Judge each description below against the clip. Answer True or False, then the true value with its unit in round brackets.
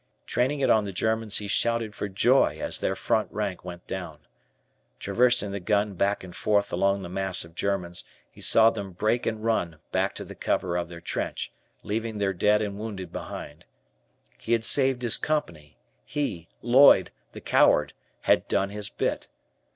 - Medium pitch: False (100 Hz)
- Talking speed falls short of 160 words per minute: False (175 wpm)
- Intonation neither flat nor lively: True (3.5 semitones)